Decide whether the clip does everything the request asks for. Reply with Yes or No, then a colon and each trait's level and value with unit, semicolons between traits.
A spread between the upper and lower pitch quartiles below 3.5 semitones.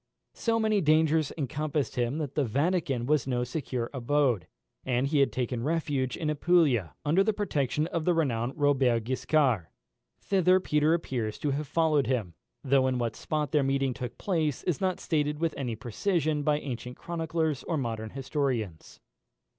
No: average, 4.1 semitones